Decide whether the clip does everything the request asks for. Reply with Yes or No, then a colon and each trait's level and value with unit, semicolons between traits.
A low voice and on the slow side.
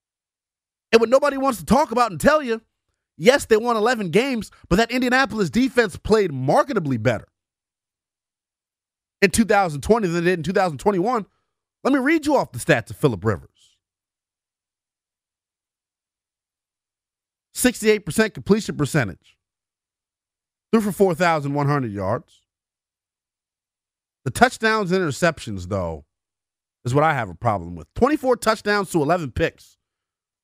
Yes: low, 125 Hz; slow, 125 wpm